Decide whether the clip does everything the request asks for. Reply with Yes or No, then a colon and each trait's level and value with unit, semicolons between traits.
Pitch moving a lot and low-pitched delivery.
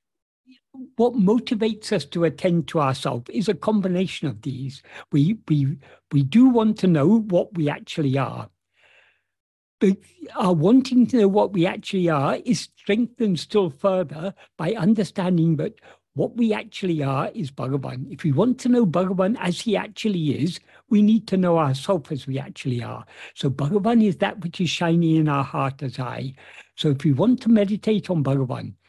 No: wide, 6.5 semitones; medium, 180 Hz